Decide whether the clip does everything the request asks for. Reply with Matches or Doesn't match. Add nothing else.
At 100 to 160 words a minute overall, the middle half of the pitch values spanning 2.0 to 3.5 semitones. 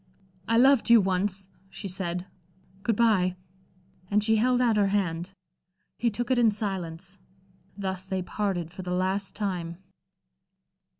Matches